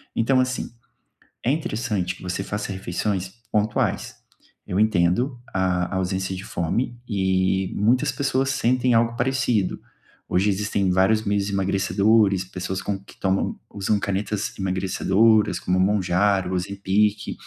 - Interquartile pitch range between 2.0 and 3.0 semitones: Yes, average, 2.7 semitones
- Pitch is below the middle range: Yes, low, 100 Hz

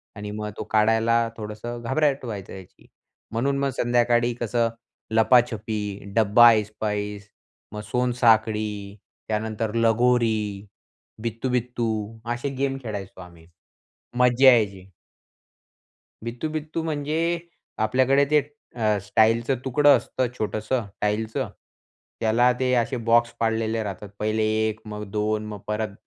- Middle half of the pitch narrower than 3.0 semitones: Yes, narrow, 2.6 semitones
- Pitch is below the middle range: Yes, low, 115 Hz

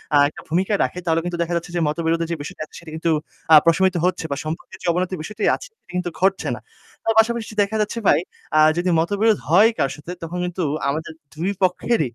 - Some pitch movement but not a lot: Yes, average, 3.1 semitones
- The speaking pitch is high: No, medium, 175 Hz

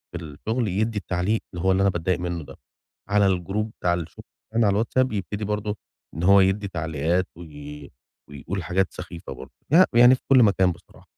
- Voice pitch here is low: Yes, very low, 95 Hz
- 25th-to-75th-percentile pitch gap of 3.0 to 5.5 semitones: Yes, average, 3.5 semitones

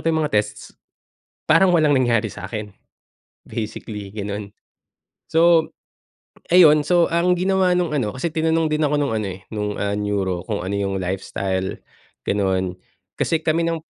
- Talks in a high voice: No, low, 120 Hz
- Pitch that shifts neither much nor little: No, wide, 8.3 semitones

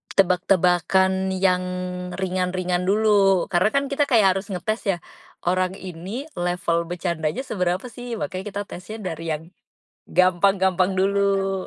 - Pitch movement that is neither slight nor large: No, narrow, 1.8 semitones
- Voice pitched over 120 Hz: Yes, high, 190 Hz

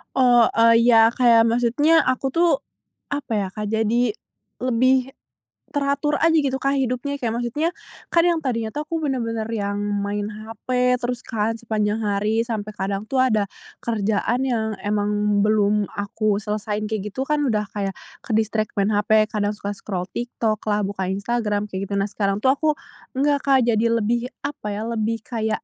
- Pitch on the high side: Yes, high, 225 Hz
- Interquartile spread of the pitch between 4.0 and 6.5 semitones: No, average, 3.3 semitones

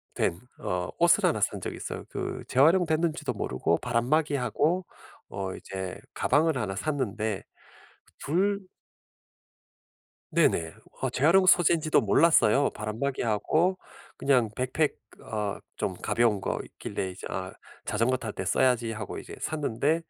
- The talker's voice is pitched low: Yes, low, 125 Hz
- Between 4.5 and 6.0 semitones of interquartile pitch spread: No, wide, 6.9 semitones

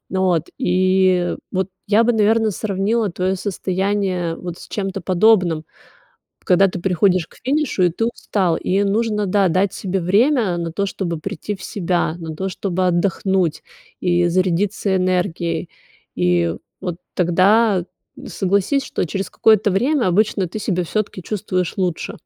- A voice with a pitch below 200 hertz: Yes, high, 190 Hz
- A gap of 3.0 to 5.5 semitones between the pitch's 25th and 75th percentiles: No, narrow, 2.6 semitones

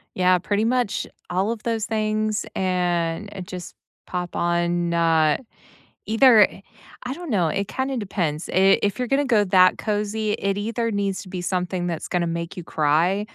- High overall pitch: Yes, high, 195 Hz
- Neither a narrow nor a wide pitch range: Yes, average, 3.6 semitones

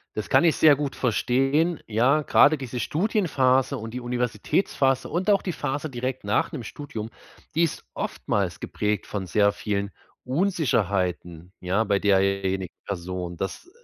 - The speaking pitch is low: Yes, low, 120 Hz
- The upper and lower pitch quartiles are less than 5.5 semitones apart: No, wide, 6.6 semitones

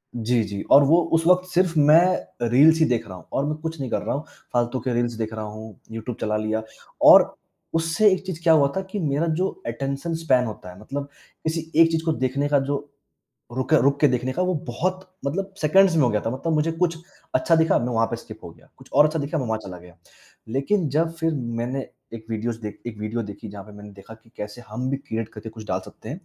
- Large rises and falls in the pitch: Yes, wide, 6.4 semitones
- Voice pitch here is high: No, low, 135 Hz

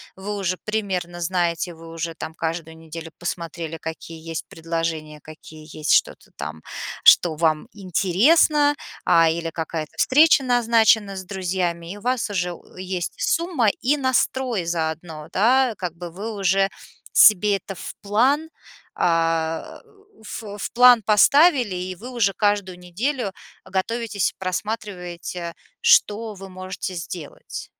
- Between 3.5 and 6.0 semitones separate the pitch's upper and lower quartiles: Yes, average, 4.6 semitones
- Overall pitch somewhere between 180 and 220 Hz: Yes, medium, 185 Hz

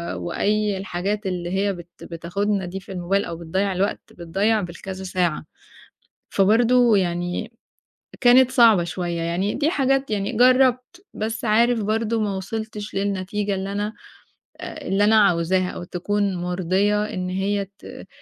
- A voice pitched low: No, high, 200 Hz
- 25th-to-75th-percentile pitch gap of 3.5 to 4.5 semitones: No, average, 3.1 semitones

